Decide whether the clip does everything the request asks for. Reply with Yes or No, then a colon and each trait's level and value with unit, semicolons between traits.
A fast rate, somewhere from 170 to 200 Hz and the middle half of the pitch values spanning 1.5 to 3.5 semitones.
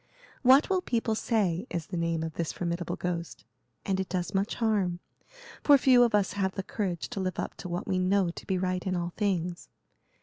Yes: fast, 210 wpm; medium, 185 Hz; average, 3.1 semitones